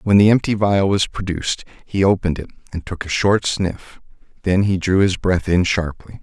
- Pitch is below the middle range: Yes, very low, 95 Hz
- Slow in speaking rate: No, average, 200 wpm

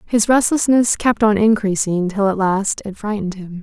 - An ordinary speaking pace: Yes, average, 180 wpm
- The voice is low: No, high, 205 Hz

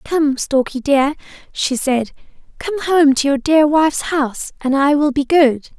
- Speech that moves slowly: No, average, 175 wpm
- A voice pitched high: Yes, very high, 285 Hz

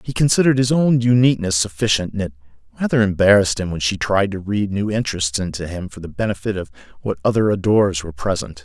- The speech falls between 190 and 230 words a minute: Yes, average, 200 wpm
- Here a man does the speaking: Yes, male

